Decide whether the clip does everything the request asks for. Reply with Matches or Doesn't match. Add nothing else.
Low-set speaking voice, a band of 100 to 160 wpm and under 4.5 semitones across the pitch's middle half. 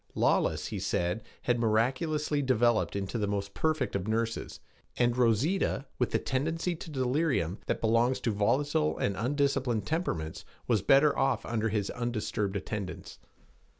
Doesn't match